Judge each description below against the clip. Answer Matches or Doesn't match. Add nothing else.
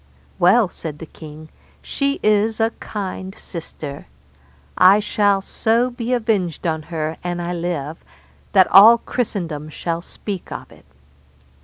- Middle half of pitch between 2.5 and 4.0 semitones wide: Doesn't match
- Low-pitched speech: Doesn't match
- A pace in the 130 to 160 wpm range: Matches